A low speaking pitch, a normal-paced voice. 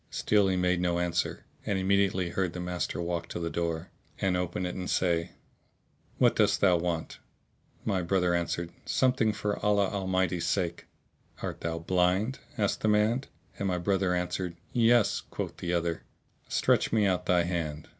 Yes: very low, 90 Hz; average, 165 wpm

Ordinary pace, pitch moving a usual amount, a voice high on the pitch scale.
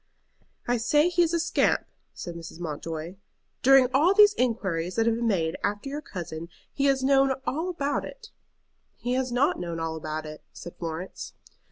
No: average, 180 wpm; wide, 8.9 semitones; high, 235 Hz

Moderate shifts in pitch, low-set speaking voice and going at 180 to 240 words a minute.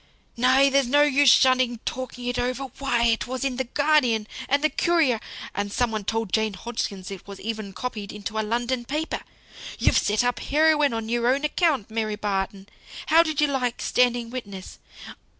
No: average, 3.9 semitones; high, 245 Hz; average, 185 wpm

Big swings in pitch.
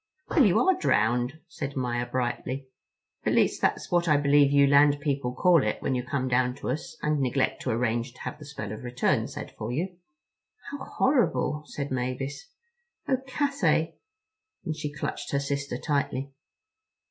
No: average, 3.2 semitones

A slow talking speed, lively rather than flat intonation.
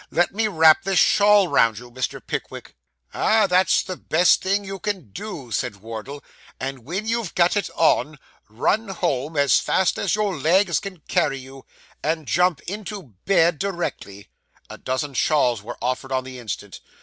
No: average, 170 wpm; wide, 7.0 semitones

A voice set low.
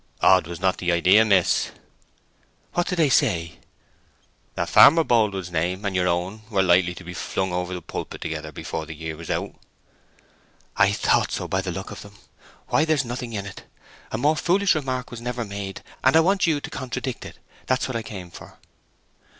Yes: low, 100 Hz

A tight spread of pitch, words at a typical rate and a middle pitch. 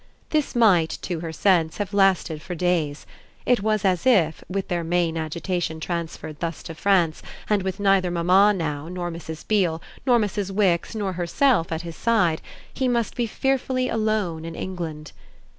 No: average, 4.0 semitones; average, 170 wpm; medium, 180 Hz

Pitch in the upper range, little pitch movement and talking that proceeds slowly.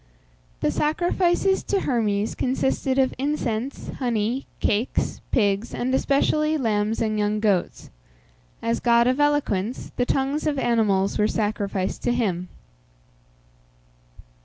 No: high, 235 Hz; average, 4.6 semitones; slow, 115 wpm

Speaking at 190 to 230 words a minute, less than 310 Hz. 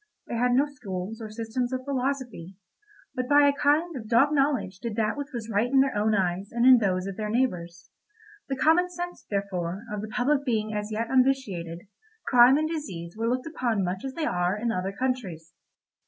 Yes: average, 200 wpm; high, 235 Hz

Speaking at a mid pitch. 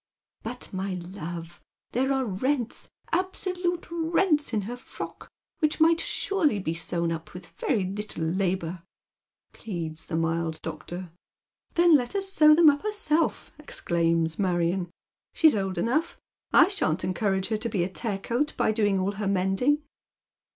No: high, 200 Hz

